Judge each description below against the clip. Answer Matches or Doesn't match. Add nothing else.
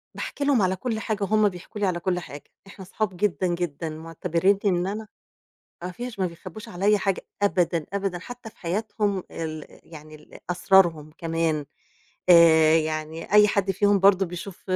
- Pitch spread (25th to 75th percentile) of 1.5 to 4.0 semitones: Matches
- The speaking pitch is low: Doesn't match